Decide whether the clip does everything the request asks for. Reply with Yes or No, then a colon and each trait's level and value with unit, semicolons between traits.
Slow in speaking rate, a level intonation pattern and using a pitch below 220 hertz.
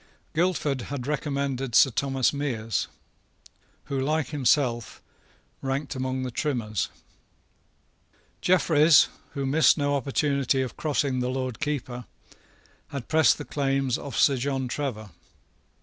Yes: slow, 120 wpm; narrow, 2.2 semitones; low, 135 Hz